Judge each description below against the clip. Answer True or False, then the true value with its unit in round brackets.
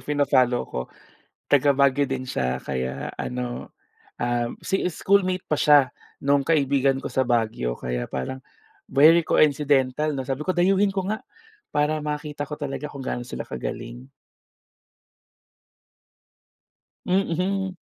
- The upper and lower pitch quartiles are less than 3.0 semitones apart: False (3.6 semitones)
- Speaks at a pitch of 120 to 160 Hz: True (140 Hz)